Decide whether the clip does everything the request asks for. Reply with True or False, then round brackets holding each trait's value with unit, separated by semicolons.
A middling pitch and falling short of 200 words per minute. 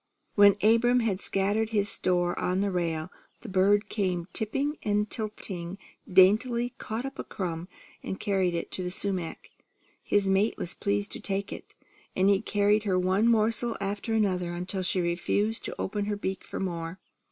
False (200 Hz; 175 wpm)